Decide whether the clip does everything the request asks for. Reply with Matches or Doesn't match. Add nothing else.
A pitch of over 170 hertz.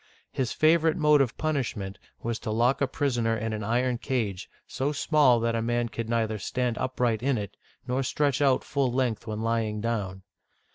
Doesn't match